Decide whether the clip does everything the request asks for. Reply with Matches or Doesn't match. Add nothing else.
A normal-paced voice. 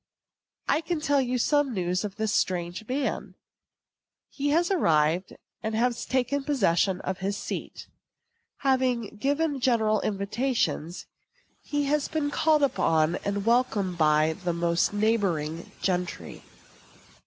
Doesn't match